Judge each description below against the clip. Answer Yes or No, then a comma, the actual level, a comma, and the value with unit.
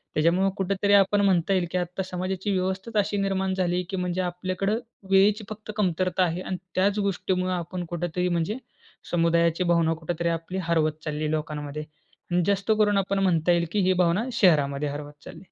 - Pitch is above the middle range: No, medium, 180 Hz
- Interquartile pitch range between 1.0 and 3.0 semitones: Yes, narrow, 2.4 semitones